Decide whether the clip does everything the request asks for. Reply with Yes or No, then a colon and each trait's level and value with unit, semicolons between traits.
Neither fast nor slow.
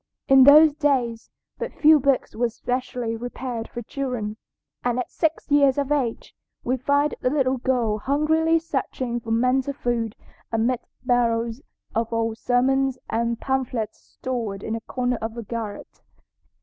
Yes: average, 150 wpm